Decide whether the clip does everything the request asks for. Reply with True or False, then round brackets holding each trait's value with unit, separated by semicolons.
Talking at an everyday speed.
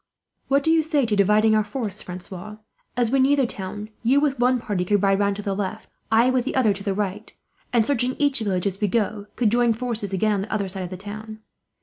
False (250 wpm)